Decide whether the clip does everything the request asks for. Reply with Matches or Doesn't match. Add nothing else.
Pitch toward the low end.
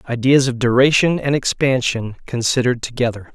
Matches